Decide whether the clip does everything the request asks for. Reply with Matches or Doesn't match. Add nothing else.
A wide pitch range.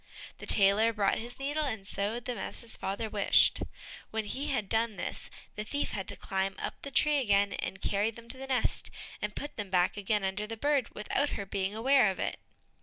Doesn't match